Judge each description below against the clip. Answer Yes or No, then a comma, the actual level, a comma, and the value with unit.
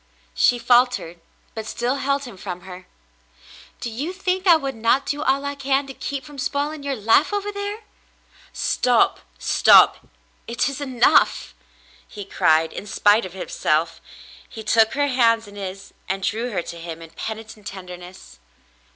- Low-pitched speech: No, high, 235 Hz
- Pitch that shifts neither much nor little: No, wide, 6.3 semitones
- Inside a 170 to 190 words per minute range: Yes, average, 175 wpm